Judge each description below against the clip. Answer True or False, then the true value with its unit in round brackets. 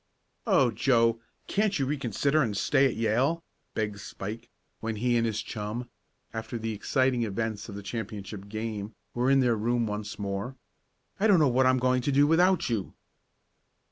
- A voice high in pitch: False (115 Hz)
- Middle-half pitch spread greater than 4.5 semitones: False (3.7 semitones)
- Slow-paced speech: False (170 wpm)